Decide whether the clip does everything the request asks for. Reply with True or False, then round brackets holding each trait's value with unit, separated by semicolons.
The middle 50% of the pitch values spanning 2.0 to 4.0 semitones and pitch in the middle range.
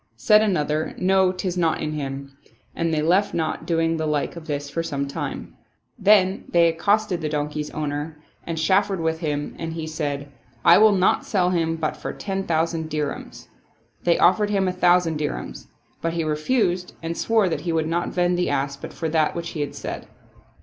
True (3.1 semitones; 165 Hz)